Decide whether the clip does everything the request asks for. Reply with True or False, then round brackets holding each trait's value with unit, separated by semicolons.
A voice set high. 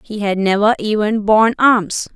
True (215 Hz)